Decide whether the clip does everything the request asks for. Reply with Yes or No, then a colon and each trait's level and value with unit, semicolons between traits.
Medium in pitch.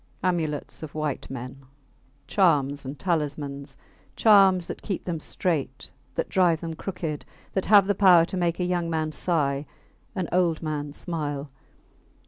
Yes: medium, 160 Hz